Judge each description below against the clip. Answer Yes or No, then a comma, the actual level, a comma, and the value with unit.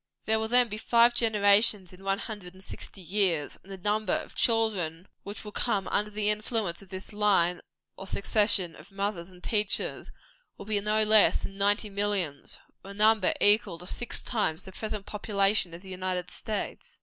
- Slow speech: No, average, 185 wpm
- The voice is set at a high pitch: Yes, high, 205 Hz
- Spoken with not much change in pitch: Yes, narrow, 2.3 semitones